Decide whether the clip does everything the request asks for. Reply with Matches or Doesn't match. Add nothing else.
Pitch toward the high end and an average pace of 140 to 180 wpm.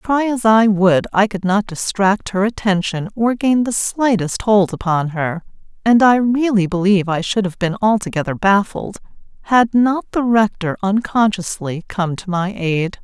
Matches